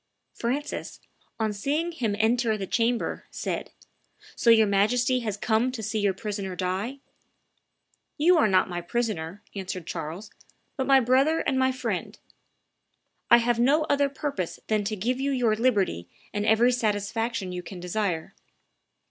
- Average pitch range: Yes, average, 4.3 semitones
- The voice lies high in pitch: Yes, high, 220 Hz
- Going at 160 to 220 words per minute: No, average, 150 wpm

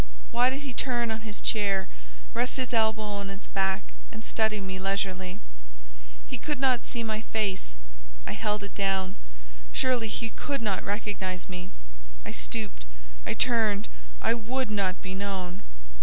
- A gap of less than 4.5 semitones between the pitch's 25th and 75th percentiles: Yes, average, 3.2 semitones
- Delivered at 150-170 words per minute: Yes, average, 155 wpm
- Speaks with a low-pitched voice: No, high, 210 Hz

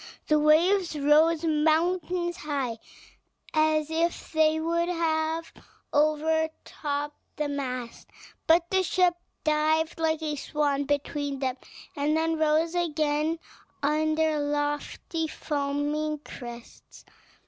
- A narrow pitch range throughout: Yes, narrow, 1.8 semitones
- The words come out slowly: Yes, slow, 105 wpm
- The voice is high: Yes, very high, 310 Hz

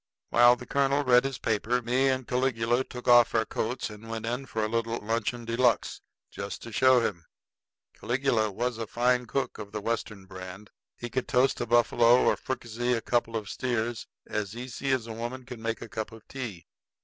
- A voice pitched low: Yes, low, 120 Hz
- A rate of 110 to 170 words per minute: No, average, 200 wpm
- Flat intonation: Yes, narrow, 1.9 semitones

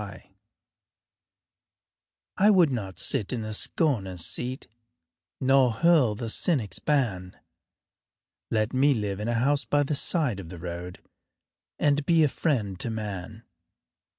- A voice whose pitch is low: Yes, low, 120 Hz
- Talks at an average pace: No, slow, 130 wpm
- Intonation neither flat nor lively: No, wide, 6.3 semitones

